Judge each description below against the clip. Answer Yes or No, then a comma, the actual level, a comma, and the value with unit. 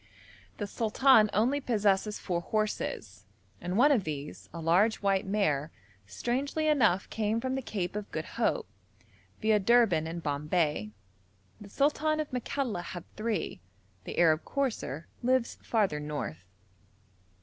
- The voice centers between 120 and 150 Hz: No, high, 210 Hz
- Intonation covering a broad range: Yes, wide, 6.6 semitones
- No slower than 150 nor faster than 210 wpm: No, slow, 135 wpm